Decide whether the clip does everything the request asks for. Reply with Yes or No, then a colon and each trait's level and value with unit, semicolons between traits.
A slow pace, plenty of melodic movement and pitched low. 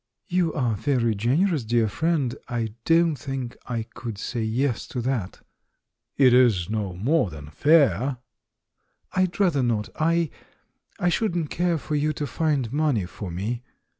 No: average, 155 wpm; wide, 5.9 semitones; low, 130 Hz